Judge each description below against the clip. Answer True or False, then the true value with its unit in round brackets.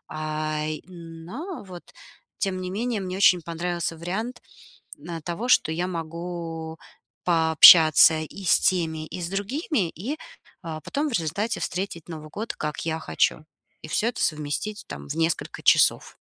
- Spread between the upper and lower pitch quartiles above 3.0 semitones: True (3.5 semitones)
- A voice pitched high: False (170 Hz)